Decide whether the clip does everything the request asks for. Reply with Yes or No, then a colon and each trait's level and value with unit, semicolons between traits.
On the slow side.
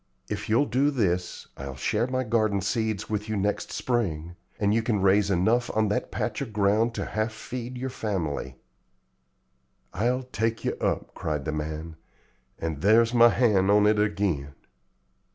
No: average, 165 wpm